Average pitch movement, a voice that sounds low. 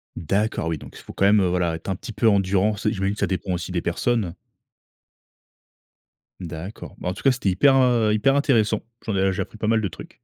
Yes: average, 3.3 semitones; low, 100 Hz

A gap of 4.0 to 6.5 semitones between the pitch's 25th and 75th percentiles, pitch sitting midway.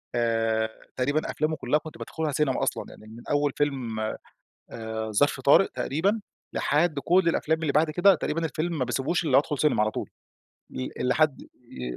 Yes: average, 5.1 semitones; medium, 145 Hz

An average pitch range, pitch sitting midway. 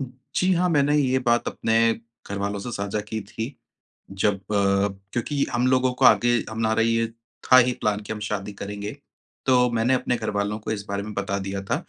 No: average, 3.6 semitones; low, 110 Hz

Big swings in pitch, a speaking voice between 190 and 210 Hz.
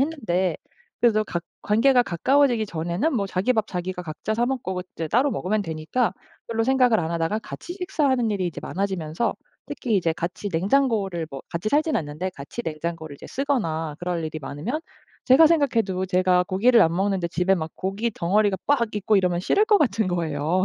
Yes: wide, 5.9 semitones; high, 195 Hz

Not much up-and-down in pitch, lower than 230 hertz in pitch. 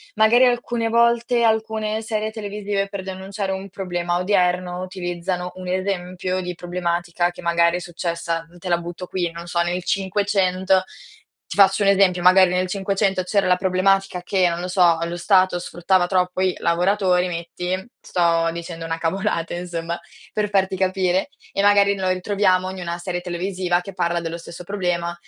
Yes: narrow, 2.0 semitones; medium, 185 Hz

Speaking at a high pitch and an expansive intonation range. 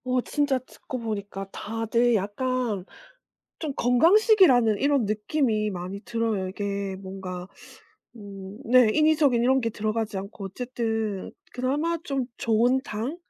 No: high, 230 Hz; average, 4.1 semitones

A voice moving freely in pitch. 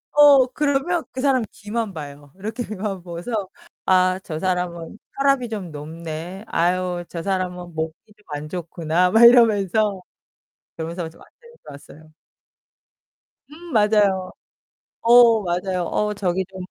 No: average, 4.8 semitones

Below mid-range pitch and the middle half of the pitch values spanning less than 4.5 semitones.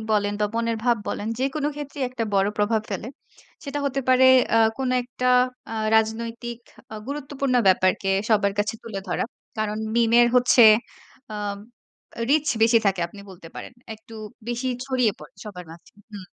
No: high, 230 Hz; average, 3.6 semitones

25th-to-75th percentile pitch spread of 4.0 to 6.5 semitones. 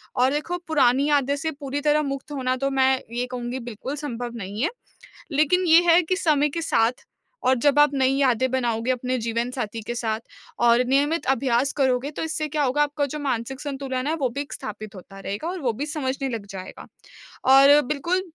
No: average, 3.4 semitones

